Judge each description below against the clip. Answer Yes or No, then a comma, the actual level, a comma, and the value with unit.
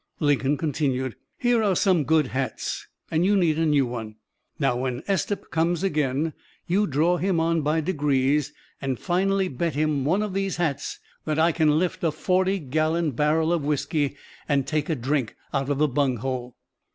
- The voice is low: No, medium, 155 Hz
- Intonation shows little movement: No, average, 3.9 semitones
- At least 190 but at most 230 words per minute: No, average, 175 wpm